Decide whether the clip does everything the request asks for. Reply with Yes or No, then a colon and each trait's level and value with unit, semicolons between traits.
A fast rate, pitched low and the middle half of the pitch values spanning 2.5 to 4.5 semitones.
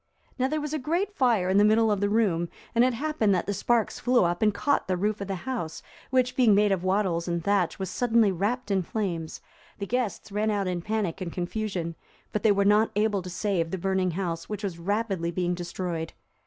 No: fast, 225 wpm; high, 200 Hz; average, 3.8 semitones